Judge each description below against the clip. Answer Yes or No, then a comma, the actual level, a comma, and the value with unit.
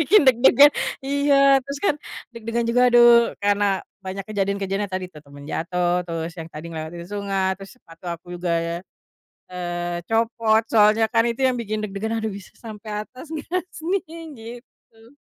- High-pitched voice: Yes, high, 215 Hz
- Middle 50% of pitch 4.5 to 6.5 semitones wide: Yes, average, 4.9 semitones